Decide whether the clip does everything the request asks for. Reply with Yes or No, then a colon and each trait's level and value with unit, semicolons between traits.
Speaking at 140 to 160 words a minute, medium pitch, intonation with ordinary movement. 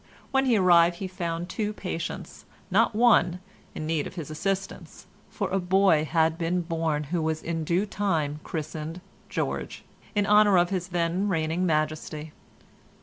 Yes: average, 155 wpm; medium, 170 Hz; average, 3.2 semitones